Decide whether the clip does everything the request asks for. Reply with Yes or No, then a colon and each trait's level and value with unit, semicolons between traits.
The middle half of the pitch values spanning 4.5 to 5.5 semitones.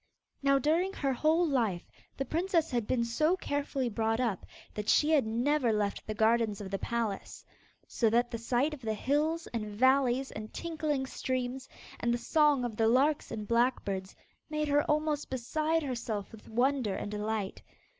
Yes: average, 4.9 semitones